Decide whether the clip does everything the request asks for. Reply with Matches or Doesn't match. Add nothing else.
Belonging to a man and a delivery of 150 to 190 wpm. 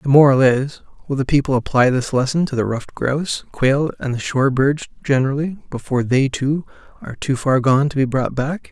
Doesn't match